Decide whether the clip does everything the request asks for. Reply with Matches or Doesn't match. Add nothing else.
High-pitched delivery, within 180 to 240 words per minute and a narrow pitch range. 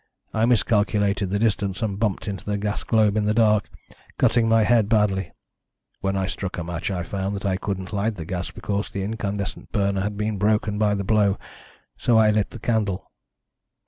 Doesn't match